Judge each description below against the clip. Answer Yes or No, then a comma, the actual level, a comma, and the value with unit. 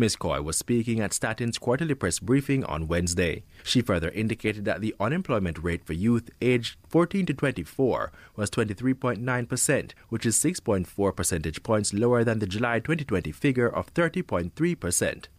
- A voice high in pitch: No, low, 115 Hz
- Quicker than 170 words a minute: No, average, 150 wpm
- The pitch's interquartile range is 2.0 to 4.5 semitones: No, average, 5.2 semitones